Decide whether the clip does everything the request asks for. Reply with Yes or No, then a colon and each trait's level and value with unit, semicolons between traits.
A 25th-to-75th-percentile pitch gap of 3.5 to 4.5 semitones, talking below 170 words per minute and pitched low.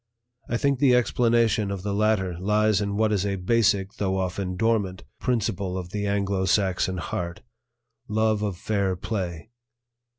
No: narrow, 2.6 semitones; average, 155 wpm; low, 100 Hz